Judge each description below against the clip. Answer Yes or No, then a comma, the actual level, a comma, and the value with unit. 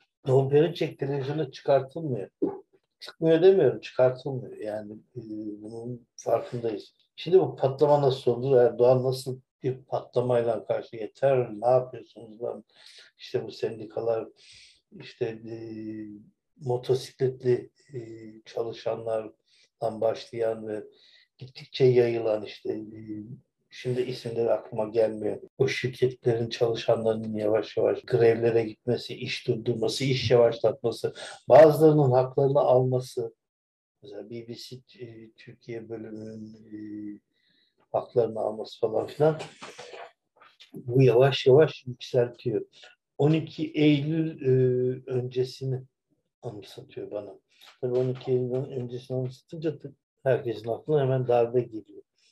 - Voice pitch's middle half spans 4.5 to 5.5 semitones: No, average, 3.2 semitones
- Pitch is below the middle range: Yes, low, 125 Hz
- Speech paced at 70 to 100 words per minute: Yes, slow, 95 wpm